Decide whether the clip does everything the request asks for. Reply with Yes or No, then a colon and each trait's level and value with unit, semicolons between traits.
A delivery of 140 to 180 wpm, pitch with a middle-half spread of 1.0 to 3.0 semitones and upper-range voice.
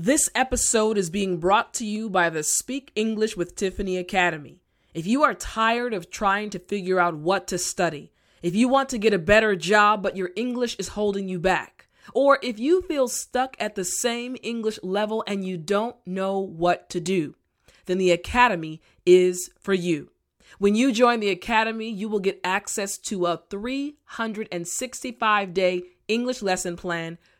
No: average, 175 wpm; average, 4.2 semitones; high, 200 Hz